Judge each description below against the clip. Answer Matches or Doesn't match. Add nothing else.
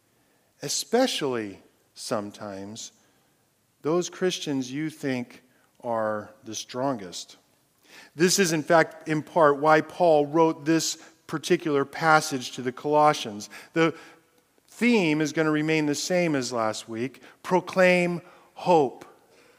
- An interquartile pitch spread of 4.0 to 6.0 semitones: Matches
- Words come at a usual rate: Doesn't match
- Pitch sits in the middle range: Matches